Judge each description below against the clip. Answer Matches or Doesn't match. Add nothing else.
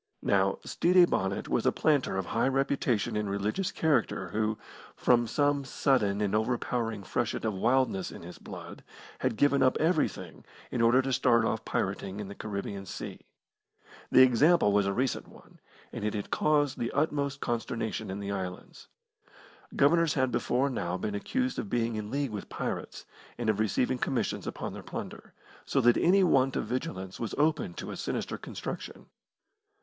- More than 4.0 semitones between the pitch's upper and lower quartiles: Matches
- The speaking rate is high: Doesn't match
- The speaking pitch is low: Matches